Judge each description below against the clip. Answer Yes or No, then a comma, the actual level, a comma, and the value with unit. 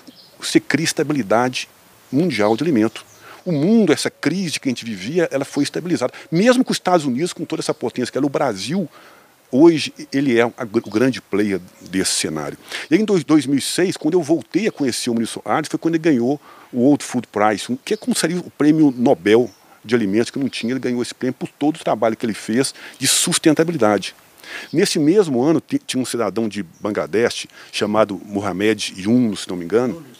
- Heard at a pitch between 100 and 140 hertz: Yes, low, 135 Hz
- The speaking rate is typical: No, fast, 200 wpm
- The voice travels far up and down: Yes, wide, 6.4 semitones